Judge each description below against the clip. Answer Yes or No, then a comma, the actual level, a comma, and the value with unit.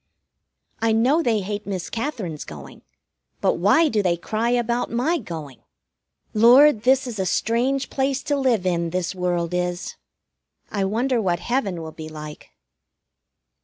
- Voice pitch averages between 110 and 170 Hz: No, high, 215 Hz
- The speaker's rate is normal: Yes, average, 150 wpm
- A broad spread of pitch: Yes, wide, 5.9 semitones